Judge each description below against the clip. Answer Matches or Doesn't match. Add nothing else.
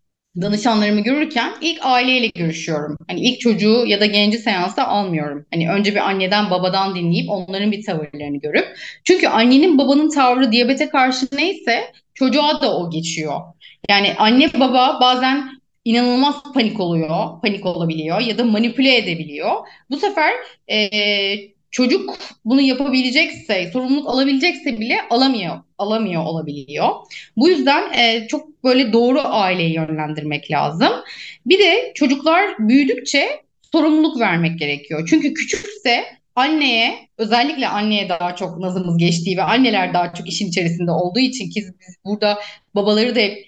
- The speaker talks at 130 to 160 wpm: Matches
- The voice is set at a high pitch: Matches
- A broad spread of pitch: Matches